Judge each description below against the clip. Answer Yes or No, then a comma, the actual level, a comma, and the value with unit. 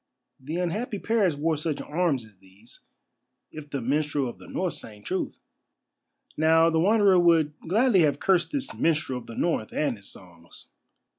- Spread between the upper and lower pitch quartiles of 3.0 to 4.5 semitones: No, wide, 5.5 semitones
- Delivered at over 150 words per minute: Yes, average, 165 wpm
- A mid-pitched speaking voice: Yes, medium, 155 Hz